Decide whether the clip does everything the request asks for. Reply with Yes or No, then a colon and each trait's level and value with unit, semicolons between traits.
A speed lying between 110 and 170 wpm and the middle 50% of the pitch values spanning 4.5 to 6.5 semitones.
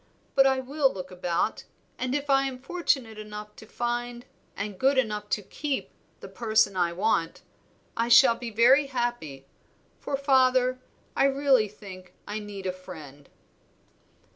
Yes: average, 150 wpm; average, 4.8 semitones